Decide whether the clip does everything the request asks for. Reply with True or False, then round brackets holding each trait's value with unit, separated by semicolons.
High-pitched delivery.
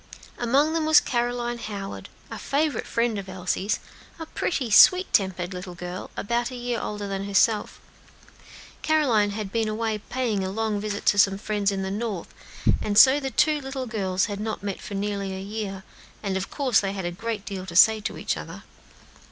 True (210 Hz)